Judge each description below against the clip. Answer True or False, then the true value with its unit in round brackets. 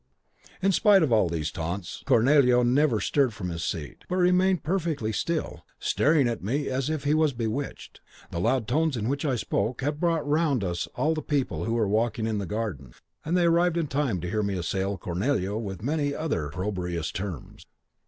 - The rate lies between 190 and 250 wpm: True (195 wpm)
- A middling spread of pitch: False (7.7 semitones)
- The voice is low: True (120 Hz)